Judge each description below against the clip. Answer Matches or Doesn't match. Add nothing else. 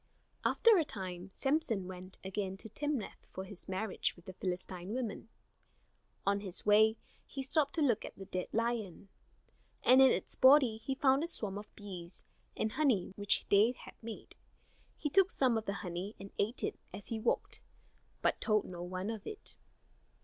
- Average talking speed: Matches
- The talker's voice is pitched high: Matches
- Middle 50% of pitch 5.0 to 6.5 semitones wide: Matches